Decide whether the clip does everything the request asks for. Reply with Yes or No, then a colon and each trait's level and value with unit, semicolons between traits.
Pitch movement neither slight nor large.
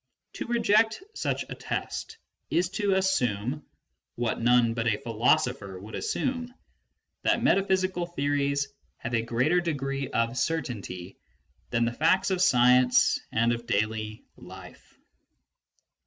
No: wide, 7.5 semitones